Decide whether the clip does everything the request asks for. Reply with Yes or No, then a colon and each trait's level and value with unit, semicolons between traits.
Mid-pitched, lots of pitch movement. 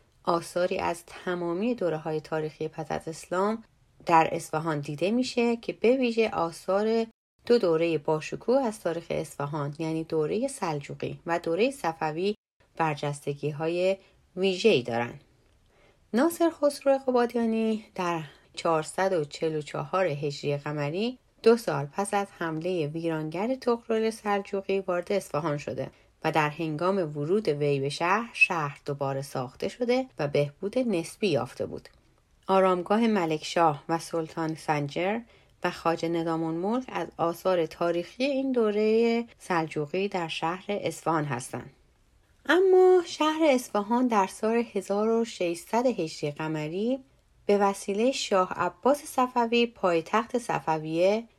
Yes: medium, 175 Hz; wide, 5.9 semitones